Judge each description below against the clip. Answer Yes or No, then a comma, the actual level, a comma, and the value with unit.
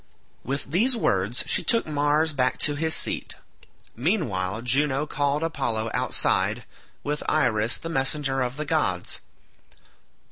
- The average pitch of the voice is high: No, medium, 145 Hz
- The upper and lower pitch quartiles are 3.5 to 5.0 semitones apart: Yes, average, 4.1 semitones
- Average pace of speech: No, slow, 130 wpm